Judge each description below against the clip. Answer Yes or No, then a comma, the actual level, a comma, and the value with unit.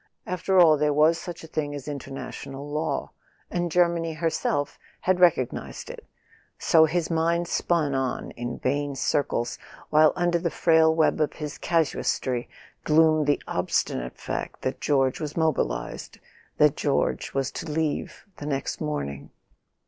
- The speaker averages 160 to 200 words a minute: No, average, 150 wpm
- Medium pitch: Yes, medium, 155 Hz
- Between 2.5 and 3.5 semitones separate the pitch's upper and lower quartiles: Yes, average, 2.8 semitones